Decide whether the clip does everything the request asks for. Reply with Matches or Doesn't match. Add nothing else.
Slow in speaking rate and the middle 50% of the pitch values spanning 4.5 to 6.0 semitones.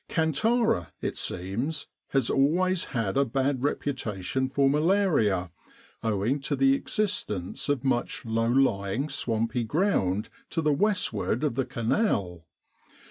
Matches